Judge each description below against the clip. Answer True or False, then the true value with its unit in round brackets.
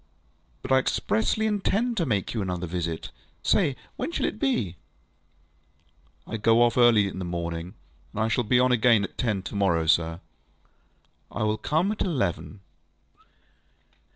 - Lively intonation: True (5.9 semitones)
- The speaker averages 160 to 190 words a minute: True (165 wpm)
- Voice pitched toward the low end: True (105 Hz)